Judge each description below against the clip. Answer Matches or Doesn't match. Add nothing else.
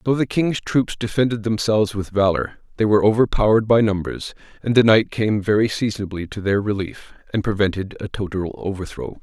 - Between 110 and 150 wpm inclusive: Doesn't match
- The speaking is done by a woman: Doesn't match